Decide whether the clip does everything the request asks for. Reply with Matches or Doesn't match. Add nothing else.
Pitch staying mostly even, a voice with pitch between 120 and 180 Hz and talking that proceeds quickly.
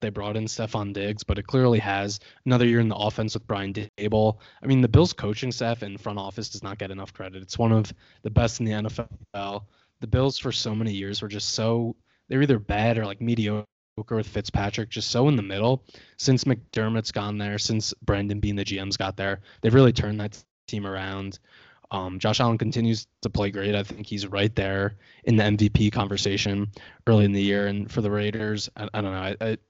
Doesn't match